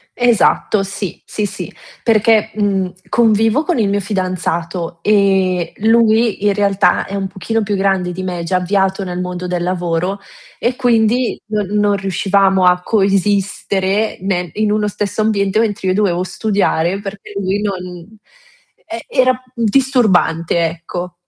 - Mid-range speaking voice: No, high, 200 Hz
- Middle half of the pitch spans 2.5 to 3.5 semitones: Yes, average, 2.8 semitones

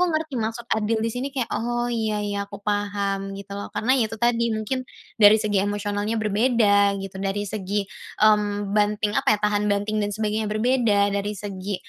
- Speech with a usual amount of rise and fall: No, narrow, 1.5 semitones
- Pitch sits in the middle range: No, high, 210 Hz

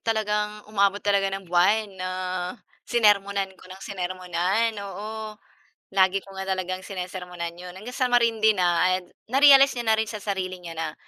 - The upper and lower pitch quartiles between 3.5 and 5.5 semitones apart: No, average, 2.8 semitones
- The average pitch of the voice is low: No, high, 195 Hz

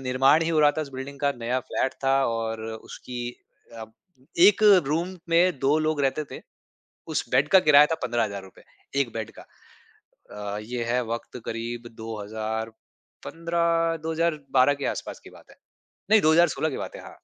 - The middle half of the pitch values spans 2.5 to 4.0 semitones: No, wide, 5.4 semitones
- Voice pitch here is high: No, low, 135 Hz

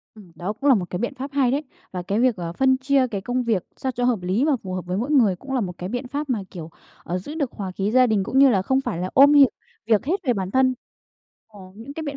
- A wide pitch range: Yes, wide, 5.9 semitones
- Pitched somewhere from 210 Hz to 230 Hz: No, high, 240 Hz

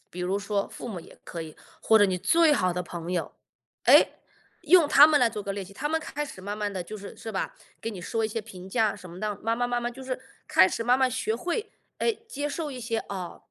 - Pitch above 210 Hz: Yes, high, 220 Hz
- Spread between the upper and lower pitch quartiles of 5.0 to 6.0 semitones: Yes, wide, 5.5 semitones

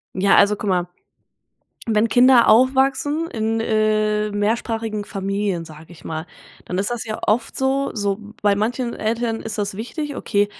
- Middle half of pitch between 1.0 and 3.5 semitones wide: Yes, average, 2.9 semitones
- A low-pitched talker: No, high, 215 Hz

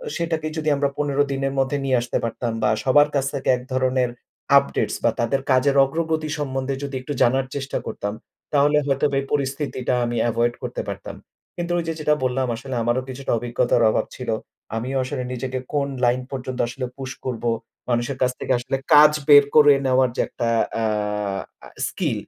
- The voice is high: No, low, 135 Hz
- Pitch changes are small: Yes, narrow, 2.2 semitones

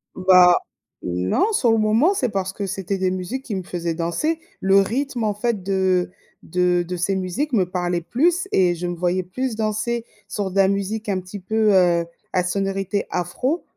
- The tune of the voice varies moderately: Yes, average, 3.5 semitones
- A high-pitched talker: Yes, high, 195 Hz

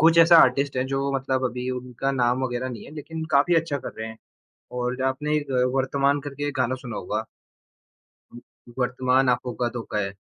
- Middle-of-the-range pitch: No, low, 130 Hz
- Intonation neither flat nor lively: No, narrow, 2.3 semitones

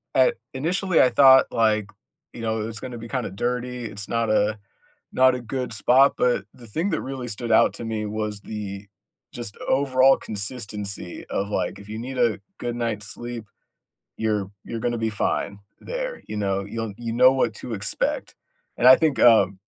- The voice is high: No, low, 115 Hz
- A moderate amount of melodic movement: Yes, average, 3.2 semitones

